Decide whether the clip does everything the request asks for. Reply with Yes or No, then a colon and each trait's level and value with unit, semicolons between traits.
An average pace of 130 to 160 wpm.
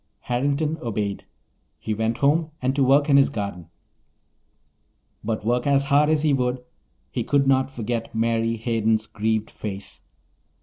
Yes: average, 145 wpm